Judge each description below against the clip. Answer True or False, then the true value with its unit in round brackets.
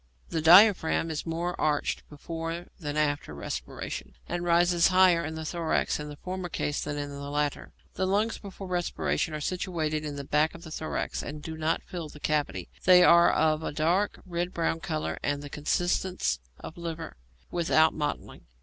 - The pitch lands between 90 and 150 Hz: False (160 Hz)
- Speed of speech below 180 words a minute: False (185 wpm)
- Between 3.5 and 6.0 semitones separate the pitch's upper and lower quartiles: False (2.8 semitones)